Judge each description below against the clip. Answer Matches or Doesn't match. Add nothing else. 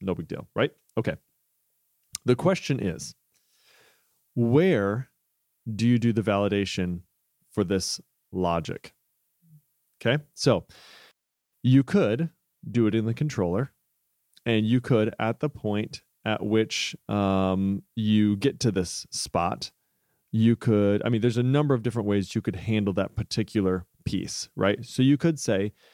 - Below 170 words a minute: Matches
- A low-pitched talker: Matches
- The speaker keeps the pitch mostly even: Doesn't match